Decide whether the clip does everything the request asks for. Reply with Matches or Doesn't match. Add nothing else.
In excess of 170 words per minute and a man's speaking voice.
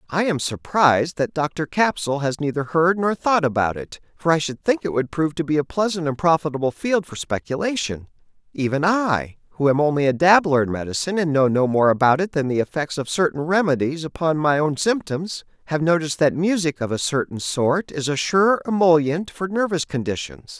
Matches